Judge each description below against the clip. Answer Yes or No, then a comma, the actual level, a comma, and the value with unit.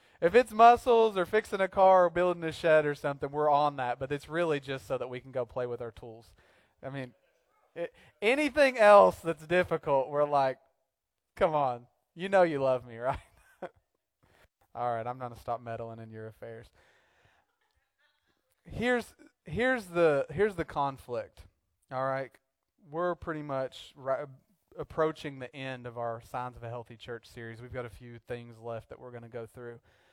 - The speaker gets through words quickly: No, average, 175 wpm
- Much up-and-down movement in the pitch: Yes, wide, 5.9 semitones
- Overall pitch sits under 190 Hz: Yes, low, 135 Hz